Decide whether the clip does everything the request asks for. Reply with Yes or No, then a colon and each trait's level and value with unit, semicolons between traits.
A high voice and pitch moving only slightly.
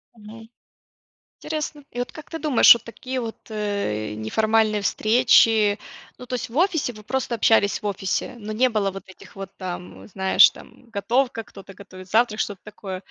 No: high, 215 Hz; average, 3.4 semitones